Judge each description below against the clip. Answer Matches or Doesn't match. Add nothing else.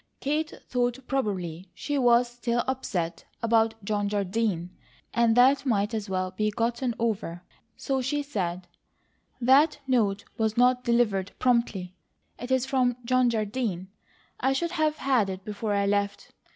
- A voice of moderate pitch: Doesn't match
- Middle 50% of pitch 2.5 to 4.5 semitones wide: Matches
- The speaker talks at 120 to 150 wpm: Matches